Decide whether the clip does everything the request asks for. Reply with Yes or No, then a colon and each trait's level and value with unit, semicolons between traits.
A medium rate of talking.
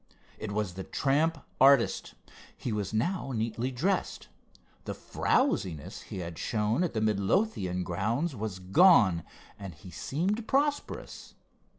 No: slow, 125 wpm